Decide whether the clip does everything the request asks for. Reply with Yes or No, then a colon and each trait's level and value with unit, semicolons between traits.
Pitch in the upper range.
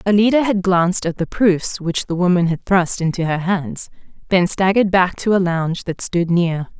No: medium, 180 Hz